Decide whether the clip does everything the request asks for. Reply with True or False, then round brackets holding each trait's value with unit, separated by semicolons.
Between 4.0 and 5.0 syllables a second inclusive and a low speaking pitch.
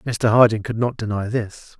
True (4.6 syllables/s; 110 Hz)